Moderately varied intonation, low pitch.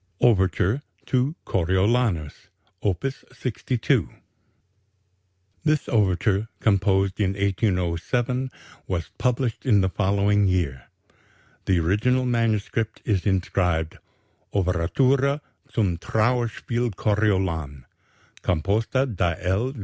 Yes: average, 4.6 semitones; low, 100 Hz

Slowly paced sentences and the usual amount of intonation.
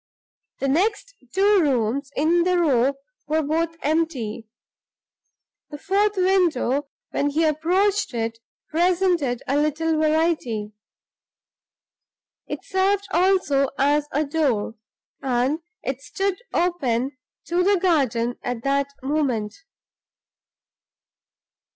Yes: slow, 100 wpm; average, 4.9 semitones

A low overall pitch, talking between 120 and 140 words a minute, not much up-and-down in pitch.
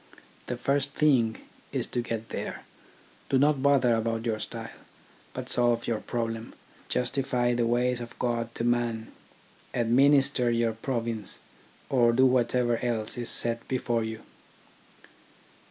Yes: low, 120 Hz; slow, 135 wpm; narrow, 1.5 semitones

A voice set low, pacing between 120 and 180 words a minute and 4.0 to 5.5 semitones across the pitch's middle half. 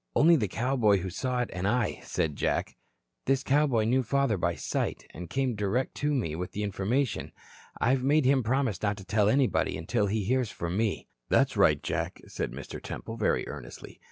No: low, 115 Hz; average, 190 wpm; average, 5.0 semitones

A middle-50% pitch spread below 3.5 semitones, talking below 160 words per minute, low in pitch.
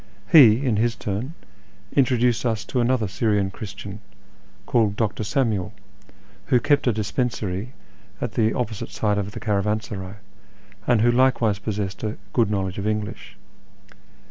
Yes: average, 2.9 semitones; average, 140 wpm; low, 110 Hz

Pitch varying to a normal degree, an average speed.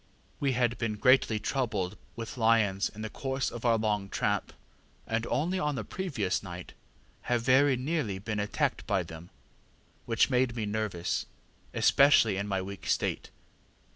Yes: average, 4.0 semitones; average, 155 wpm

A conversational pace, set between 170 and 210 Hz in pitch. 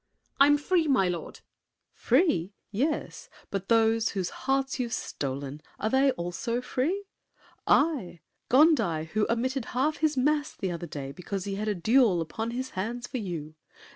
No: average, 160 wpm; high, 230 Hz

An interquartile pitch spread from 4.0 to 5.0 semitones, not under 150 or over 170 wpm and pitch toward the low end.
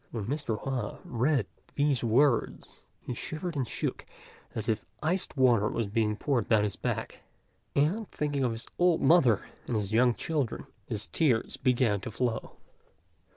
Yes: average, 4.6 semitones; average, 155 wpm; low, 125 Hz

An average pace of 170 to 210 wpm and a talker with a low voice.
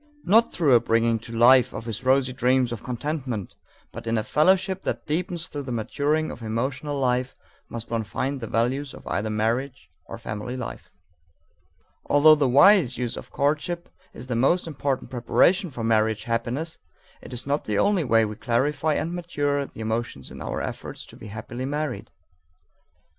Yes: average, 175 wpm; low, 130 Hz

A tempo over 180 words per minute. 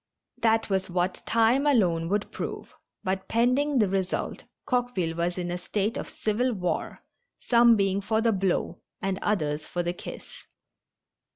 No: average, 155 wpm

